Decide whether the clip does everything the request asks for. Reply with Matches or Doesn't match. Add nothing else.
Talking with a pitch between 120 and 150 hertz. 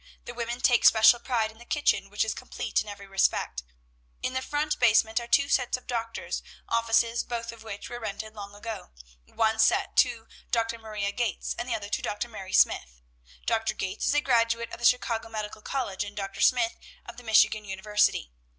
Doesn't match